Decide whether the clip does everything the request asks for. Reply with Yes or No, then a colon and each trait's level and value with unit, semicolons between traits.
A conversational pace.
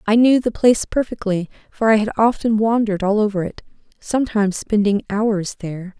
Yes: average, 170 wpm